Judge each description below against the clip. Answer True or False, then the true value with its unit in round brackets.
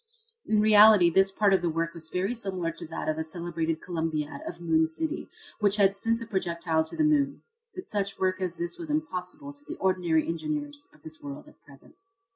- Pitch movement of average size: True (5.0 semitones)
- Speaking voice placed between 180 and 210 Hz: True (185 Hz)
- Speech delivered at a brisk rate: True (210 wpm)